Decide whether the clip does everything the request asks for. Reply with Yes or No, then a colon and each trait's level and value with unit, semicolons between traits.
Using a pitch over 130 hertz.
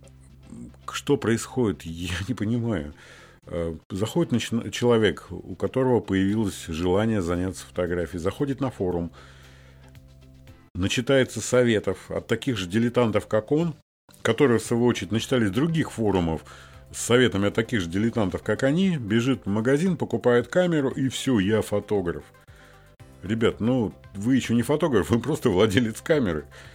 No: low, 110 Hz